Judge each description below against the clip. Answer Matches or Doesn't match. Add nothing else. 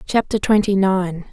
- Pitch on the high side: Matches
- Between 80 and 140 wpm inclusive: Matches